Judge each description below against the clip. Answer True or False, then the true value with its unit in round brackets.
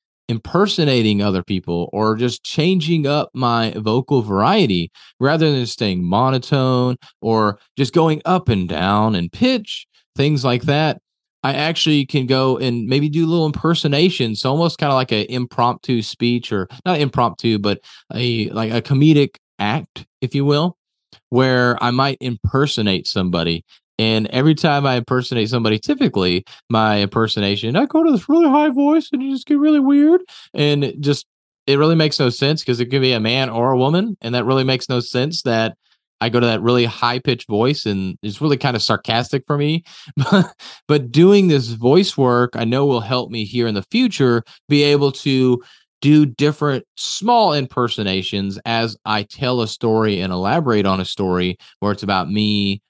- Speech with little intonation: False (5.0 semitones)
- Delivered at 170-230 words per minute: True (180 wpm)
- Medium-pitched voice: False (125 Hz)